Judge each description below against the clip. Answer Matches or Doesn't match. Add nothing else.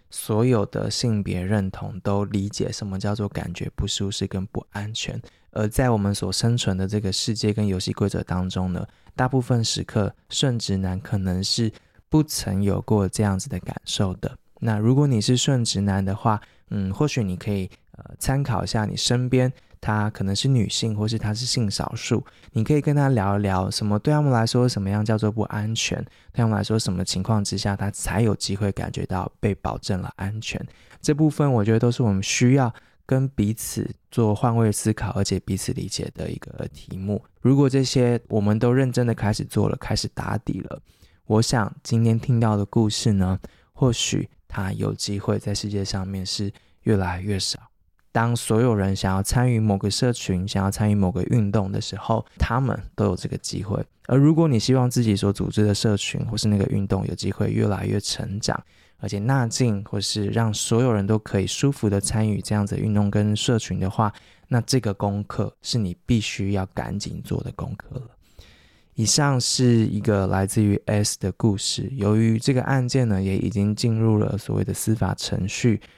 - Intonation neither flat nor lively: Matches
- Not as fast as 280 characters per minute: Doesn't match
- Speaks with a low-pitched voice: Matches